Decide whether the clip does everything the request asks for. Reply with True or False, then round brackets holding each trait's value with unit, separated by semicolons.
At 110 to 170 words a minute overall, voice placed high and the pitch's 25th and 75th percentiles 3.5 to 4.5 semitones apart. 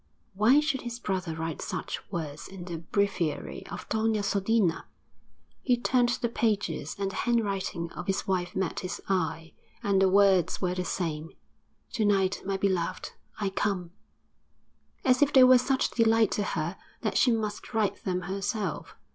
True (165 wpm; 195 Hz; 3.8 semitones)